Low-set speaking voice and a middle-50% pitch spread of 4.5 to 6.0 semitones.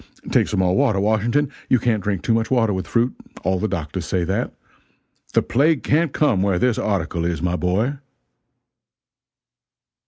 Yes: low, 105 Hz; average, 5.2 semitones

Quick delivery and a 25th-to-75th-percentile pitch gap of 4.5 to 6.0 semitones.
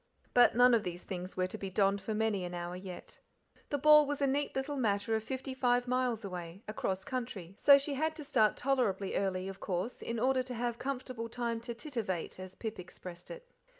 Yes: fast, 215 wpm; wide, 5.4 semitones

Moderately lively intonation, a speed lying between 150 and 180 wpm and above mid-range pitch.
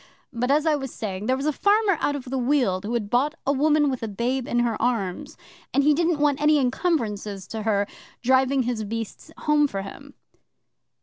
No: average, 4.8 semitones; fast, 205 wpm; very high, 255 Hz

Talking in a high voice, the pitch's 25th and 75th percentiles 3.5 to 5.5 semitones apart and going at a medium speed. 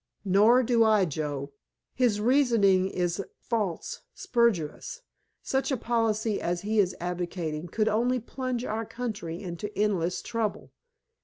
No: high, 210 Hz; average, 4.8 semitones; slow, 130 wpm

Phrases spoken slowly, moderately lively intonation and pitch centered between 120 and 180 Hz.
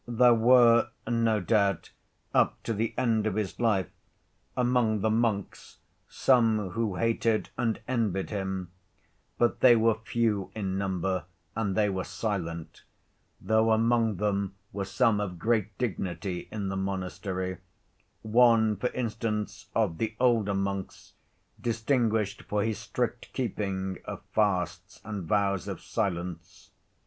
No: slow, 130 wpm; average, 3.0 semitones; low, 105 Hz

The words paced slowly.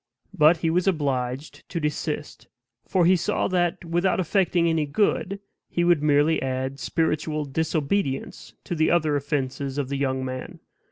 No: average, 155 wpm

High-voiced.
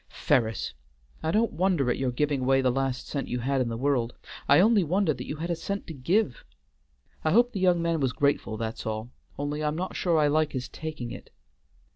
No: medium, 145 Hz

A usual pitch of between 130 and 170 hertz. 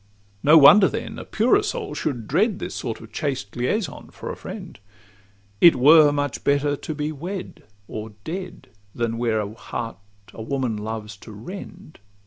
Yes: medium, 140 Hz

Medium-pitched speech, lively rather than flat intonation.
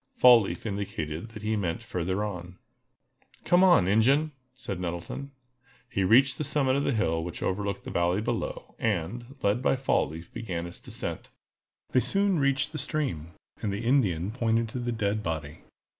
No: low, 105 Hz; wide, 6.3 semitones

